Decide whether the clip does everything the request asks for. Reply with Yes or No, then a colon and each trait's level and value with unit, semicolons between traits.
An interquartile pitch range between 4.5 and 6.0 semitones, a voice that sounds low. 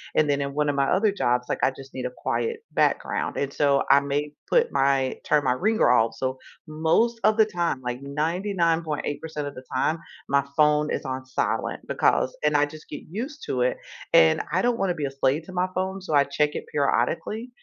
No: average, 4.9 semitones; medium, 150 Hz